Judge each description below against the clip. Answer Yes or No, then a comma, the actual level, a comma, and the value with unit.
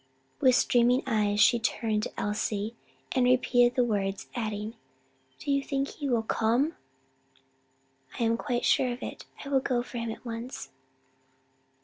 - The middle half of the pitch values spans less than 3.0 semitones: Yes, narrow, 2.5 semitones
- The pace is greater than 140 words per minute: Yes, average, 155 wpm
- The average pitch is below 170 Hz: No, high, 240 Hz